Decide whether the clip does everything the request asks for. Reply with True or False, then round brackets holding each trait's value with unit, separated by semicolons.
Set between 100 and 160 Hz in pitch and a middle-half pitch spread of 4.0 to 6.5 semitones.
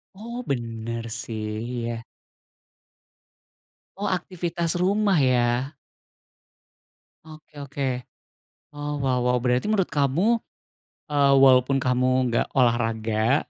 True (135 Hz; 4.5 semitones)